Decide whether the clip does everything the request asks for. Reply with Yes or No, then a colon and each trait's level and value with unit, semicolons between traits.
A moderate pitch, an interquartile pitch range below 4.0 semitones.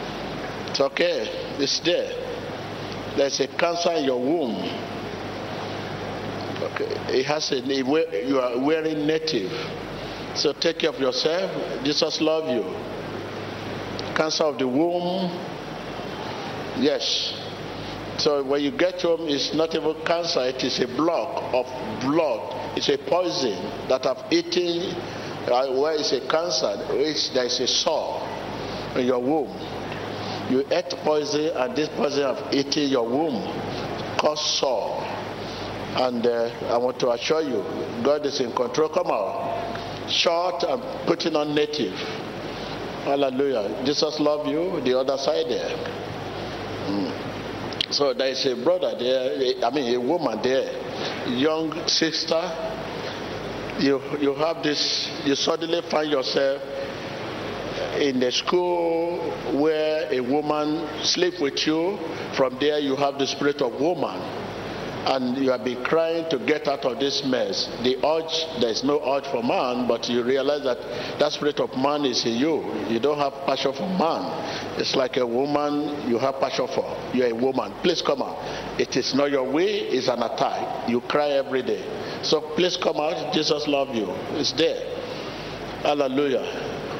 Yes: medium, 145 Hz; average, 3.3 semitones